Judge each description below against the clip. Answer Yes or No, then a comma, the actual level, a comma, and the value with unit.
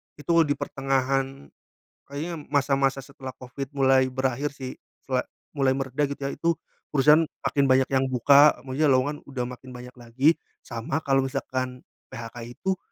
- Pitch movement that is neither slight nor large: No, narrow, 1.6 semitones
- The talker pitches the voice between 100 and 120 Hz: No, low, 135 Hz